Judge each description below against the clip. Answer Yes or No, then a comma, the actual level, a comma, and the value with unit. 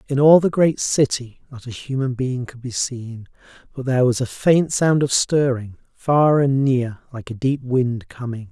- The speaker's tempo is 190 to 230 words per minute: Yes, average, 195 wpm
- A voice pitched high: No, low, 130 Hz